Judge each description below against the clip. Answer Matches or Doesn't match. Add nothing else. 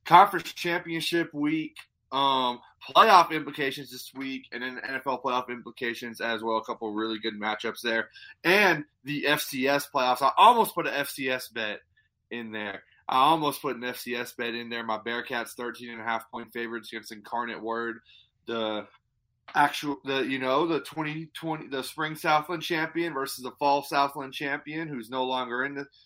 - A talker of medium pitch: Doesn't match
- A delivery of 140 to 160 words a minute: Doesn't match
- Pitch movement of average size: Matches